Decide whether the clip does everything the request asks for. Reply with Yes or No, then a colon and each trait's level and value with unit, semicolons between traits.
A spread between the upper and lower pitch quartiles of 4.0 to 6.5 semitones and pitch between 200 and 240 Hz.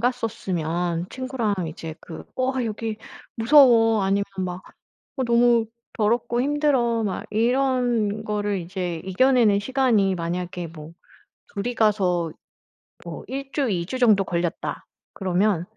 Yes: average, 5.1 semitones; high, 215 Hz